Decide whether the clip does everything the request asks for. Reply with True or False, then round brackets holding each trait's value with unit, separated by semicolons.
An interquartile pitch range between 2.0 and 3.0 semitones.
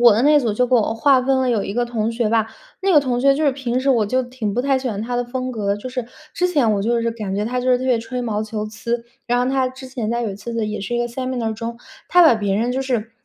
True (2.7 semitones)